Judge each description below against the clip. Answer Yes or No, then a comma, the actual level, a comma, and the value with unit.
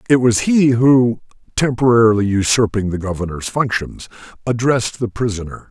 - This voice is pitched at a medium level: No, low, 115 Hz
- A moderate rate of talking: No, slow, 125 wpm